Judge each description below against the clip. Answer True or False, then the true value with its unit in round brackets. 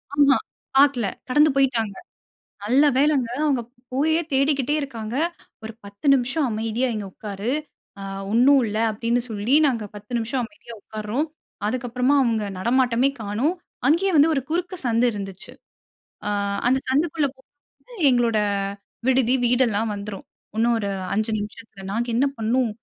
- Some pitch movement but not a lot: True (4.0 semitones)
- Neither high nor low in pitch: False (245 Hz)